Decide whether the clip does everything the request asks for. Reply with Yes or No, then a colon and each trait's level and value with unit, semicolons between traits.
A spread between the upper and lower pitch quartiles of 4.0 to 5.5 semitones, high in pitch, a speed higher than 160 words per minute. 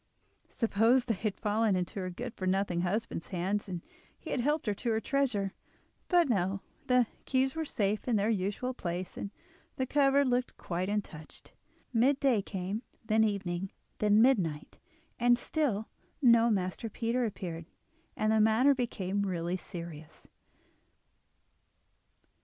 No: average, 4.7 semitones; high, 215 Hz; average, 145 wpm